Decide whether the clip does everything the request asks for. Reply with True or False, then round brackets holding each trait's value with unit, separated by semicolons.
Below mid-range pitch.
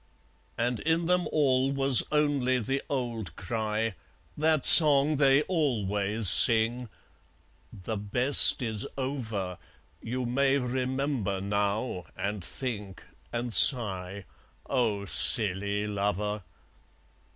True (120 Hz)